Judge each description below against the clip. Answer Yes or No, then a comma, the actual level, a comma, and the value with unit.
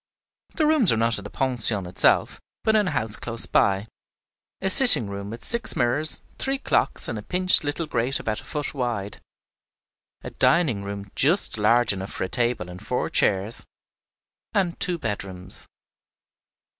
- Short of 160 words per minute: No, average, 165 wpm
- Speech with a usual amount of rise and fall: No, wide, 8.7 semitones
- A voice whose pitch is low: Yes, low, 120 Hz